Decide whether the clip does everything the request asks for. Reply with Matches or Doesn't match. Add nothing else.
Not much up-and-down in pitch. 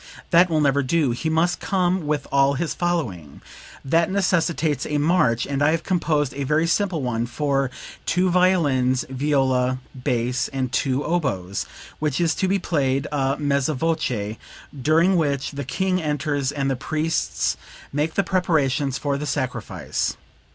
Doesn't match